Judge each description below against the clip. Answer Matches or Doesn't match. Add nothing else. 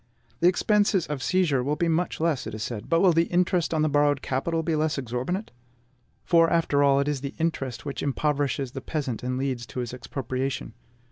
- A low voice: Doesn't match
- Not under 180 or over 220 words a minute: Matches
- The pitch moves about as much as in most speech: Matches